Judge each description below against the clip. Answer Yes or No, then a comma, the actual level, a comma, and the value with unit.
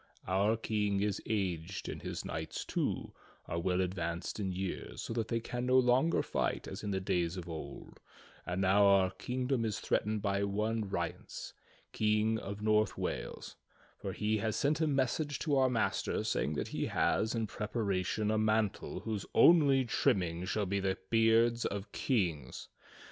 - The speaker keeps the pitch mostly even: No, average, 3.2 semitones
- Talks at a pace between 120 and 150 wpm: No, average, 170 wpm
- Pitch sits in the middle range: No, low, 105 Hz